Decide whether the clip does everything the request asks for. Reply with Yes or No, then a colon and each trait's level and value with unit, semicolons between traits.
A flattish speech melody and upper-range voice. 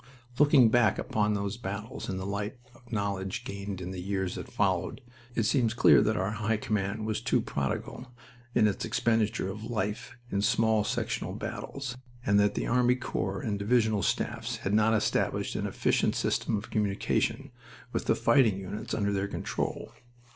No: narrow, 2.2 semitones; low, 105 Hz